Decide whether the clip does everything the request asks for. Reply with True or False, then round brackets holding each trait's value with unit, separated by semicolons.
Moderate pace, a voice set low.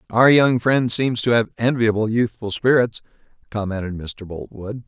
True (150 wpm; 115 Hz)